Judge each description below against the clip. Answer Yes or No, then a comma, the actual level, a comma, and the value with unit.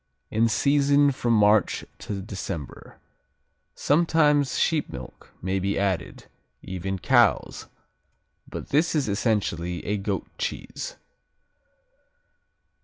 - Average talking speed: No, slow, 100 wpm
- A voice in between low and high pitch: No, low, 105 Hz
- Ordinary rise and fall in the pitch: No, wide, 6.9 semitones